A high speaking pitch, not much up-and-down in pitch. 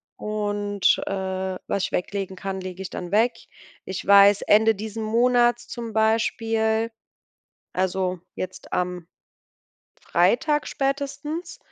No: high, 205 Hz; average, 3.3 semitones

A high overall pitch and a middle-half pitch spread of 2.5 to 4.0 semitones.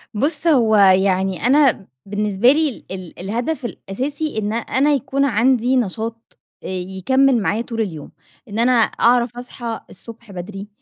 No: high, 230 Hz; average, 4.7 semitones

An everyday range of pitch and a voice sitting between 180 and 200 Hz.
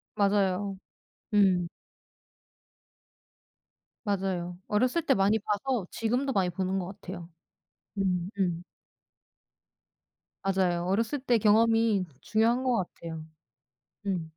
Yes: average, 3.7 semitones; high, 195 Hz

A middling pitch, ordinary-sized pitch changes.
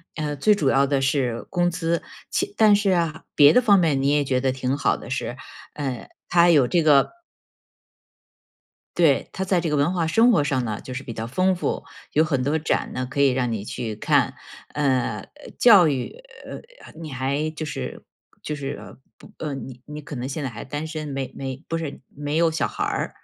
Yes: medium, 145 Hz; average, 3.7 semitones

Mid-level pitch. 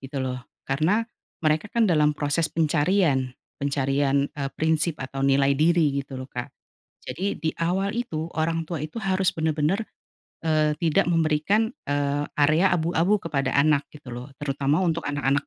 Yes: medium, 155 Hz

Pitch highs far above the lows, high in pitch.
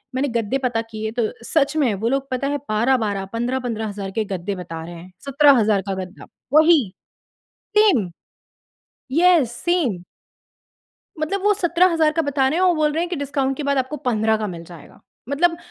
Yes: wide, 6.4 semitones; very high, 265 Hz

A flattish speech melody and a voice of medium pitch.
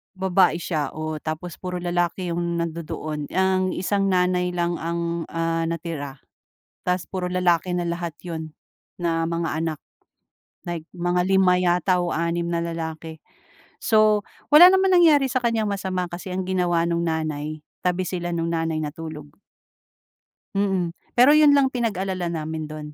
Yes: narrow, 2.2 semitones; medium, 175 Hz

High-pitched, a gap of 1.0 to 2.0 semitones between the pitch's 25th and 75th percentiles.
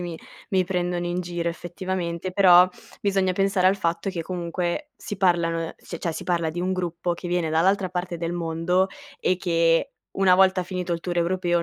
No: medium, 175 Hz; narrow, 1.6 semitones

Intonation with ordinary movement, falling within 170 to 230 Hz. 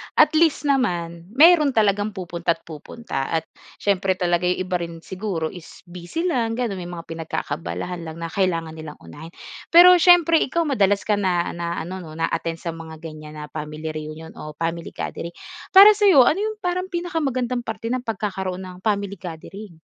No: wide, 7.0 semitones; medium, 185 Hz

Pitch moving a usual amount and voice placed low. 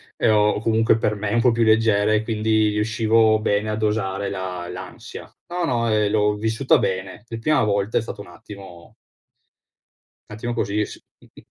No: narrow, 1.8 semitones; low, 105 Hz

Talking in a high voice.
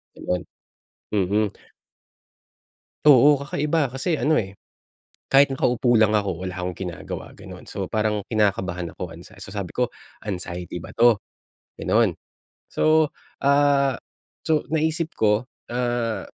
No: low, 115 Hz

